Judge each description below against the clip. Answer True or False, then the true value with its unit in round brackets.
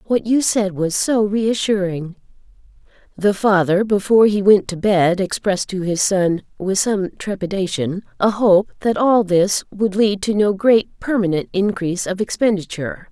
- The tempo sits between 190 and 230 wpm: False (155 wpm)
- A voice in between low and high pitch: False (195 Hz)